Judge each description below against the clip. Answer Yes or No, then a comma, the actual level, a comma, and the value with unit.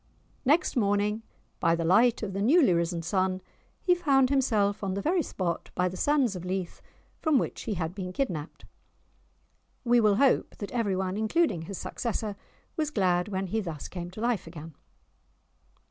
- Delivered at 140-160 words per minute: No, average, 175 wpm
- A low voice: No, high, 200 Hz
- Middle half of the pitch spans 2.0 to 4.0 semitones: No, average, 5.1 semitones